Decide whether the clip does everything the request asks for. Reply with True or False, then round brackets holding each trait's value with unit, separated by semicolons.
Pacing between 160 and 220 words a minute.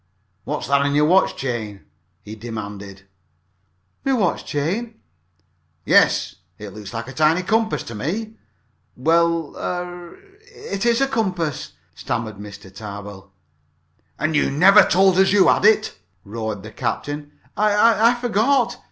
False (145 wpm)